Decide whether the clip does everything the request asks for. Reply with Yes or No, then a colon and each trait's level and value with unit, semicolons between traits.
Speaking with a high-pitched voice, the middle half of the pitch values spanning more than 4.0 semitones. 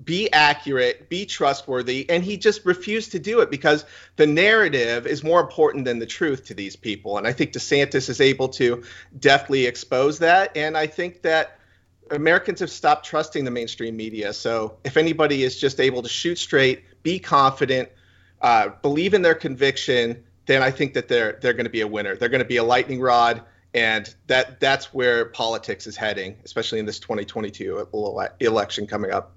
No: low, 135 Hz; average, 4.6 semitones